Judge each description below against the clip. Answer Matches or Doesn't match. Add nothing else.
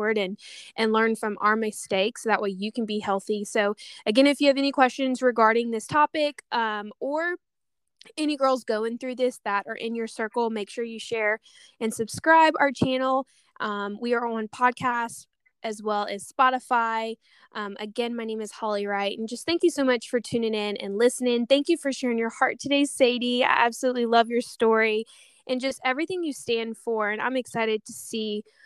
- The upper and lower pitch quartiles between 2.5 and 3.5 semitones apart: Matches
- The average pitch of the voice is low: Doesn't match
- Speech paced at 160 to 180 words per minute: Doesn't match